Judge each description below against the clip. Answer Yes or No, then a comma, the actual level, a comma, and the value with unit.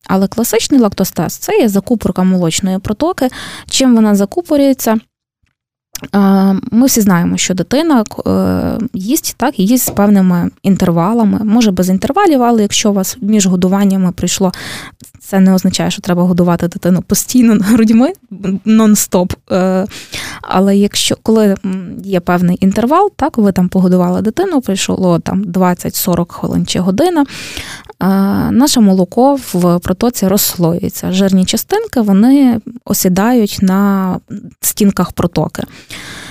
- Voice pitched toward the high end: Yes, high, 195 Hz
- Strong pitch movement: No, average, 3.8 semitones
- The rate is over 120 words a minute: No, average, 115 wpm